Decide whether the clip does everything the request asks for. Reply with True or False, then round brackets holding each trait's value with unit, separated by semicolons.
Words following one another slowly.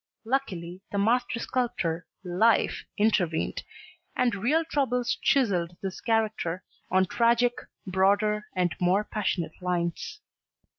True (105 wpm)